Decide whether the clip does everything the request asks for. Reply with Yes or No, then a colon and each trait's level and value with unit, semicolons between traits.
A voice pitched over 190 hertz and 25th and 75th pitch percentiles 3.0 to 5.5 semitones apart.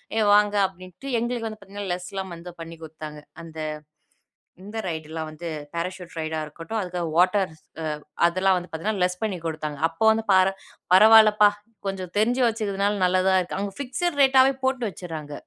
No: medium, 185 Hz; average, 4.3 semitones